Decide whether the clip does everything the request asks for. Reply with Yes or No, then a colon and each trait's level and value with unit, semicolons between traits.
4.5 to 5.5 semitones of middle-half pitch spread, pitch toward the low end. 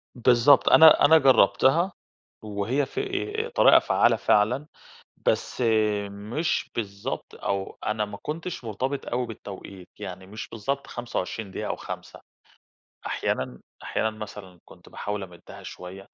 Yes: average, 5.0 semitones; low, 110 Hz